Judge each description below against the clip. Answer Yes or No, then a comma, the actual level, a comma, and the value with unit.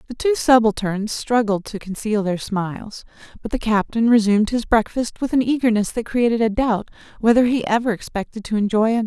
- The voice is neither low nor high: No, high, 220 Hz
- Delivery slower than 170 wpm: No, average, 185 wpm